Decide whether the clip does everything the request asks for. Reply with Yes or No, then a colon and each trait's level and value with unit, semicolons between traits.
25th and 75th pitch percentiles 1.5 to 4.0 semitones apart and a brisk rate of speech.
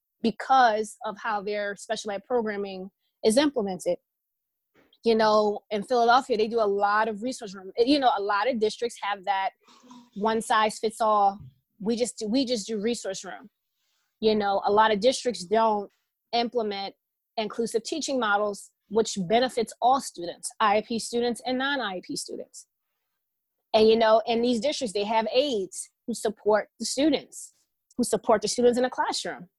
No: average, 2.9 semitones; average, 160 wpm